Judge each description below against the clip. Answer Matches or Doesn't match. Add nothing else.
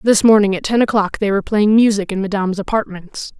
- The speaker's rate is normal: Doesn't match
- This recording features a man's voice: Doesn't match